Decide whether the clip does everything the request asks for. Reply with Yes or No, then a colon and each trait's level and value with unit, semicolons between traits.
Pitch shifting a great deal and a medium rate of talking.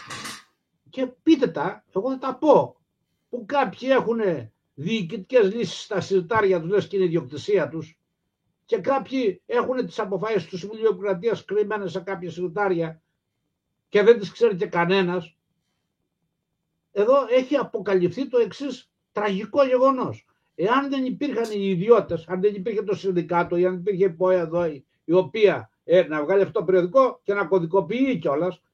No: average, 4.9 semitones; average, 150 wpm